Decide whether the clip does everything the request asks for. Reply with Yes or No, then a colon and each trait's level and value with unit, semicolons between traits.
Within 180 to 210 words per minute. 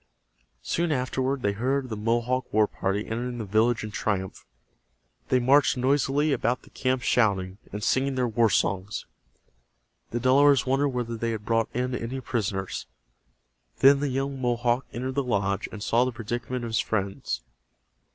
No: average, 160 wpm